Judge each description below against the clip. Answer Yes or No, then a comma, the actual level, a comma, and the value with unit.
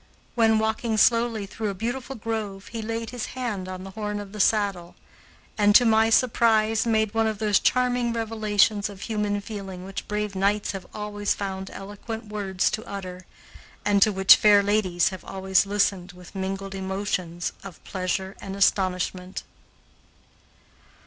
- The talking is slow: No, average, 155 wpm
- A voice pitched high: Yes, high, 205 Hz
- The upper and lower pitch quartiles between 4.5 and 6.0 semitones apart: No, narrow, 2.4 semitones